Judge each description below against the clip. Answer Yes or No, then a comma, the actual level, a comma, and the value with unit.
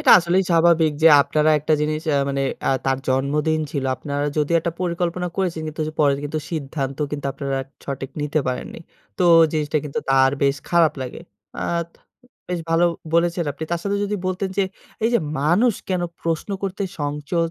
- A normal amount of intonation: Yes, average, 3.3 semitones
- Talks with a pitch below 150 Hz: No, medium, 155 Hz